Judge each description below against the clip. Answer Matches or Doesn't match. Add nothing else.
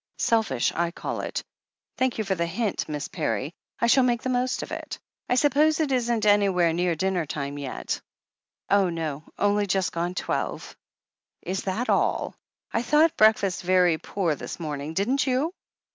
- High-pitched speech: Matches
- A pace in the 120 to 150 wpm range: Doesn't match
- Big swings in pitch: Matches